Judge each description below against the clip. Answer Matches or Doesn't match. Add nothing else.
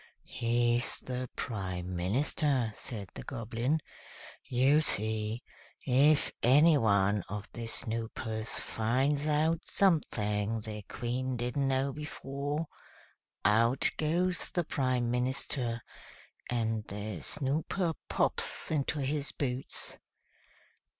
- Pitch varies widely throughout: Doesn't match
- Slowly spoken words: Matches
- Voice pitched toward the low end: Matches